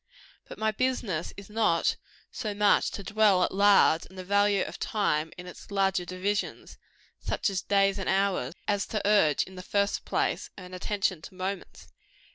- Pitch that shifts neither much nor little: No, narrow, 2.0 semitones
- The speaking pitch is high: Yes, high, 195 Hz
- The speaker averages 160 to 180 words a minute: Yes, average, 175 wpm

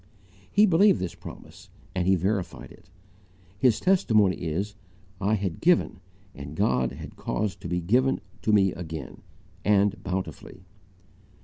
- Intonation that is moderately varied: Yes, average, 4.1 semitones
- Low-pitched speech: Yes, very low, 95 Hz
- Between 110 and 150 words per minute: Yes, slow, 135 wpm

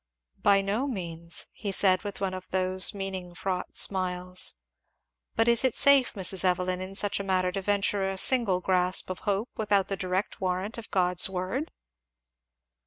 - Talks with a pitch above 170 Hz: Yes, high, 190 Hz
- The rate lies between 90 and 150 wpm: No, average, 170 wpm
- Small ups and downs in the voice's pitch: Yes, narrow, 1.8 semitones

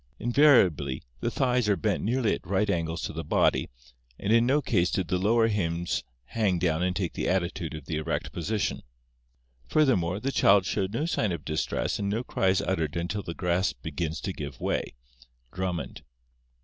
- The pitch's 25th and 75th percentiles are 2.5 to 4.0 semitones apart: No, average, 4.4 semitones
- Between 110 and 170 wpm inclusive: No, average, 185 wpm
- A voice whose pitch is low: Yes, very low, 95 Hz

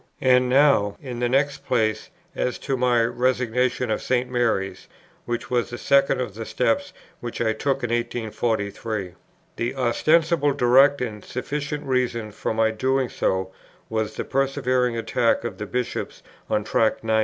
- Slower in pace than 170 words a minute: Yes, average, 155 wpm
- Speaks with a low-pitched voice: Yes, low, 120 Hz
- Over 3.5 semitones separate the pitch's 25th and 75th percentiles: No, average, 2.7 semitones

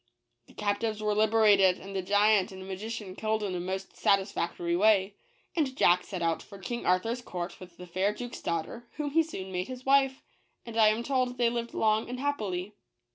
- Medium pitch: No, high, 210 Hz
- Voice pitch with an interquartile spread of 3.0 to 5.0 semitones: Yes, average, 4.0 semitones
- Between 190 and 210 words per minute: Yes, average, 200 wpm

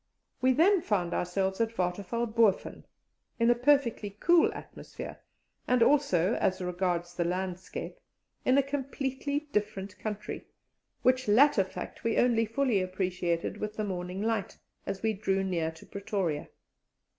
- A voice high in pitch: Yes, high, 210 Hz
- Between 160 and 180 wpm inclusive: No, average, 140 wpm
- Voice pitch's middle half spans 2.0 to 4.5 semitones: No, average, 4.9 semitones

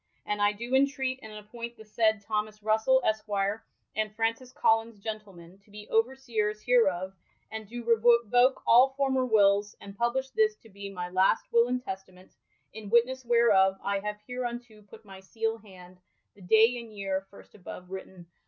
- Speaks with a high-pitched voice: Yes, high, 220 Hz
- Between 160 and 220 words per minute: Yes, average, 165 wpm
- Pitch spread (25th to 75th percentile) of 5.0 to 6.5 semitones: No, average, 3.1 semitones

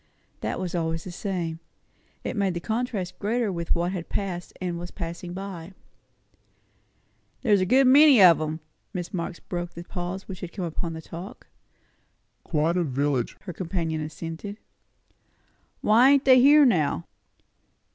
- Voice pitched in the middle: Yes, medium, 175 Hz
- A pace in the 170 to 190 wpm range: No, average, 160 wpm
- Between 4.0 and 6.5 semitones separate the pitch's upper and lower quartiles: No, average, 3.3 semitones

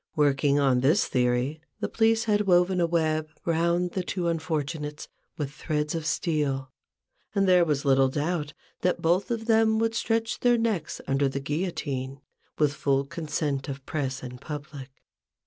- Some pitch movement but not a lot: Yes, average, 4.5 semitones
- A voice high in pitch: No, medium, 155 Hz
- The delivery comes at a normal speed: Yes, average, 160 wpm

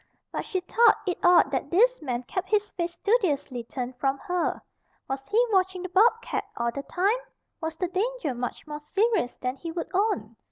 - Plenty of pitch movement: Yes, wide, 7.1 semitones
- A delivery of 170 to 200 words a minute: Yes, average, 190 wpm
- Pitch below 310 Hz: No, very high, 350 Hz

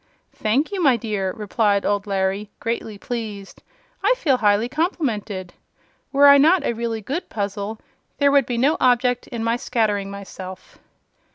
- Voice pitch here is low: No, high, 225 Hz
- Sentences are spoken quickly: No, average, 155 wpm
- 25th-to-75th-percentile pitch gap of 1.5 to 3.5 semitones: No, average, 4.5 semitones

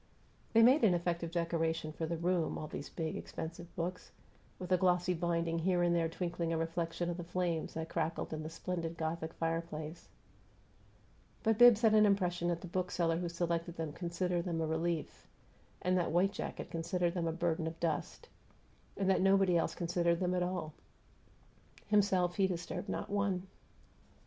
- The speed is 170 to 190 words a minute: Yes, average, 175 wpm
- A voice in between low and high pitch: Yes, medium, 170 Hz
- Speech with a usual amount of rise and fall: No, narrow, 1.7 semitones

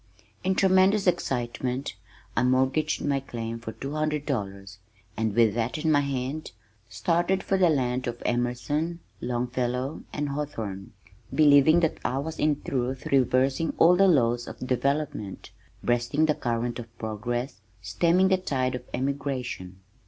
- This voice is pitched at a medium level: No, low, 130 Hz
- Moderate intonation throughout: Yes, average, 4.2 semitones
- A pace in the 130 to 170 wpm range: Yes, average, 145 wpm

